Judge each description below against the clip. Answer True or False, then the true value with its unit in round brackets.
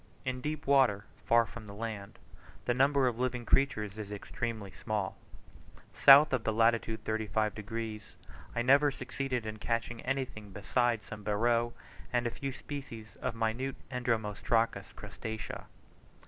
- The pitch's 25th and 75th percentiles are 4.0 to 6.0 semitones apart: False (2.8 semitones)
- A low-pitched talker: True (115 Hz)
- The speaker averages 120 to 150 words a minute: True (140 wpm)